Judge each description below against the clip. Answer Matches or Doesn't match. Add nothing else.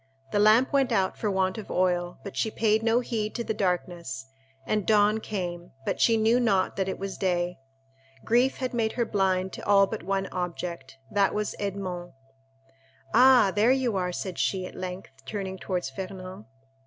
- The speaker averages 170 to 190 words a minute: Matches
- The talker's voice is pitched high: Matches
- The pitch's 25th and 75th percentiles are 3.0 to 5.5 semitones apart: Matches